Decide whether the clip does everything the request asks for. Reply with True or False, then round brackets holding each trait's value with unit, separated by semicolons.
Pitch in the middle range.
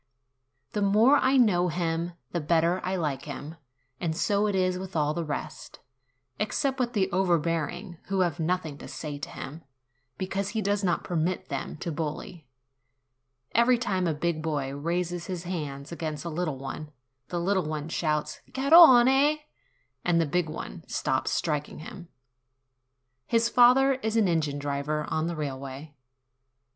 True (170 Hz)